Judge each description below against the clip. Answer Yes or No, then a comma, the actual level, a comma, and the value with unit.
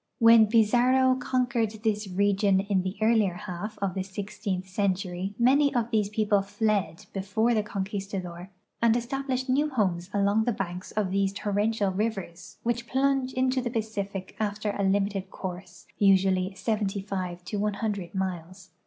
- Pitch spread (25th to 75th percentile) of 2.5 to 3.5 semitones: Yes, average, 2.9 semitones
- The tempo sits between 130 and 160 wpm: Yes, average, 145 wpm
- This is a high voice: Yes, high, 205 Hz